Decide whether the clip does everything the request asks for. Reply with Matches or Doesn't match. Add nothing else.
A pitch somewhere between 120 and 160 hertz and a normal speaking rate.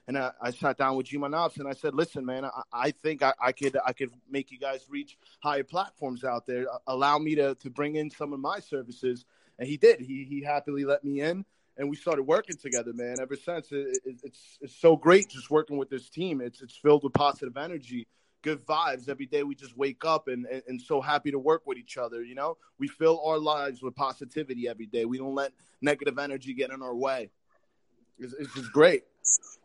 Doesn't match